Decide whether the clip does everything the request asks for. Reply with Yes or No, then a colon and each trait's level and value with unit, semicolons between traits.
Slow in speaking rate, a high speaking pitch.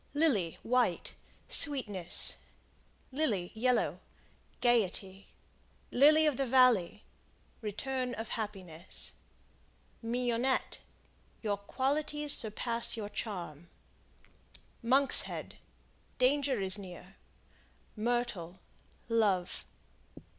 Yes: slow, 75 wpm; high, 230 Hz